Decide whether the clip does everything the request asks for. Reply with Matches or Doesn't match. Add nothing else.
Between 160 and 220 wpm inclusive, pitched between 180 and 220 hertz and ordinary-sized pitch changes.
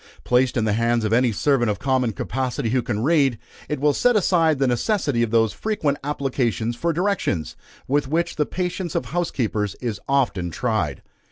Doesn't match